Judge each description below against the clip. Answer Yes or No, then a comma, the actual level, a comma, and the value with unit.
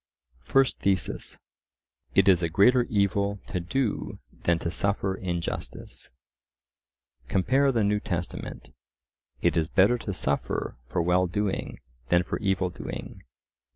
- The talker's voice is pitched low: Yes, very low, 95 Hz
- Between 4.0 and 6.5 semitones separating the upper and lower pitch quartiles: No, average, 3.0 semitones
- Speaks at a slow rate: Yes, slow, 125 wpm